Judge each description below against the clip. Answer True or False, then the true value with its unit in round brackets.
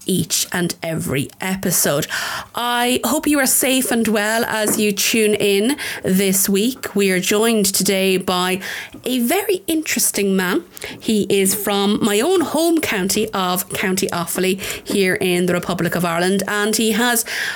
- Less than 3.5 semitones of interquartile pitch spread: False (4.0 semitones)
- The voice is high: True (205 Hz)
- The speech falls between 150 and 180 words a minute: True (155 wpm)